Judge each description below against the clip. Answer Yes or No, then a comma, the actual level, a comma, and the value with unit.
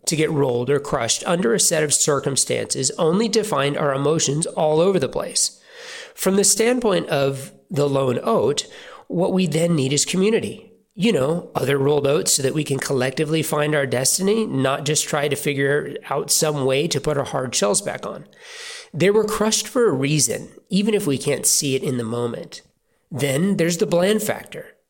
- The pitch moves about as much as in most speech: No, wide, 7.2 semitones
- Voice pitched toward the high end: No, medium, 155 Hz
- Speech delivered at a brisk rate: No, average, 195 wpm